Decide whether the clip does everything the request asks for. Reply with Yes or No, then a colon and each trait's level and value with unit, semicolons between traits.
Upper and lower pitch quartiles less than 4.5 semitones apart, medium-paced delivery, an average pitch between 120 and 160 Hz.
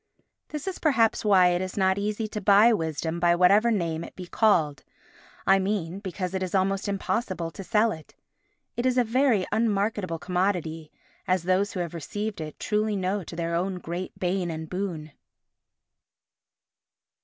No: average, 3.4 semitones; average, 165 wpm; high, 190 Hz